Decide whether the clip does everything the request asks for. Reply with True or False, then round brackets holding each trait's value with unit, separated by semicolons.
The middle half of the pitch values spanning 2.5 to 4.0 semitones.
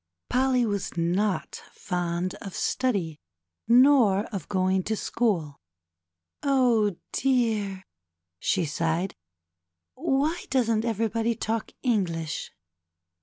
False (4.8 semitones)